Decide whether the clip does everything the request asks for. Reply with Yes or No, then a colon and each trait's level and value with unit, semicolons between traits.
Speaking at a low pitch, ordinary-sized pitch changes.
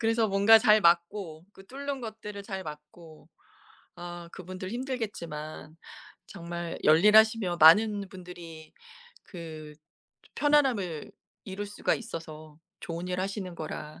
No: medium, 185 Hz; average, 4.3 semitones